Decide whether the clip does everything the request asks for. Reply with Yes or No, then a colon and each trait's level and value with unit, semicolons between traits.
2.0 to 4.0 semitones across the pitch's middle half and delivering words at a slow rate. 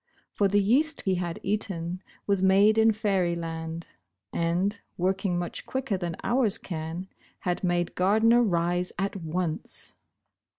Yes: average, 3.0 semitones; slow, 130 wpm